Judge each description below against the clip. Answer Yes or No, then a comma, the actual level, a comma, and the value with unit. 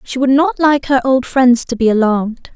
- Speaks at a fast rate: Yes, fast, 235 wpm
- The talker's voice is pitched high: Yes, very high, 260 Hz